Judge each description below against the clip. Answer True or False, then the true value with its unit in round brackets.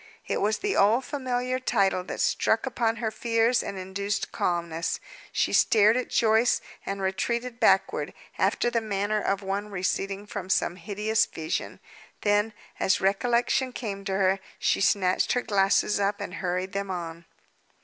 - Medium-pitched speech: False (205 Hz)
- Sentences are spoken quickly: False (155 wpm)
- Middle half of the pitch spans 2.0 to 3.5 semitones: True (3.1 semitones)